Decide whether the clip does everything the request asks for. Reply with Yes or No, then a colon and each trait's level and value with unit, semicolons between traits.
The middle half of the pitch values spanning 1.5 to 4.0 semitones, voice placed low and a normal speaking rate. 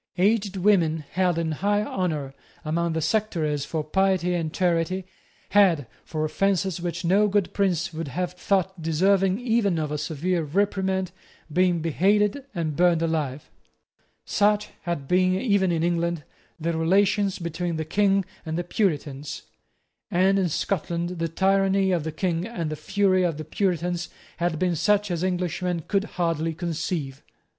No: average, 3.1 semitones; medium, 175 Hz; average, 150 wpm